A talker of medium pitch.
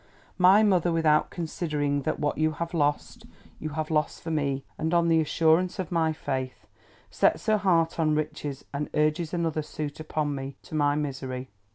Yes: medium, 155 Hz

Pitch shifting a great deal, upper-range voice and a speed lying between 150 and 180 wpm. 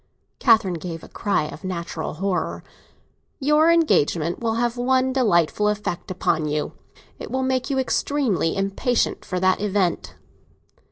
No: wide, 6.7 semitones; high, 205 Hz; slow, 135 wpm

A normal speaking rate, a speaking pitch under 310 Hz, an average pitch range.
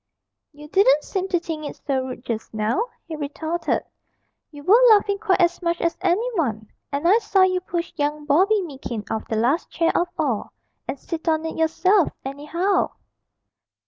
No: average, 175 wpm; very high, 325 Hz; average, 4.5 semitones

